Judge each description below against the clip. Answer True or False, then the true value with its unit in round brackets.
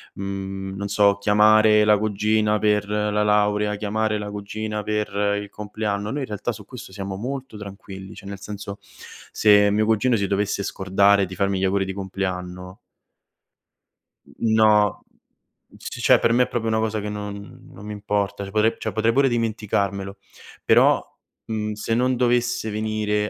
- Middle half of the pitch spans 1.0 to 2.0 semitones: True (1.5 semitones)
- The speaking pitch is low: True (105 Hz)